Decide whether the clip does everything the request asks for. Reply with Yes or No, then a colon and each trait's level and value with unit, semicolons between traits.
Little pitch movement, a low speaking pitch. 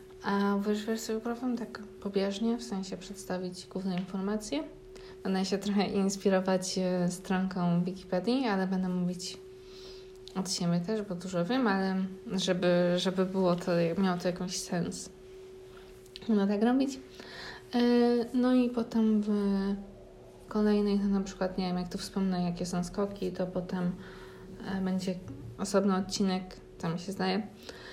No: narrow, 2.3 semitones; high, 190 Hz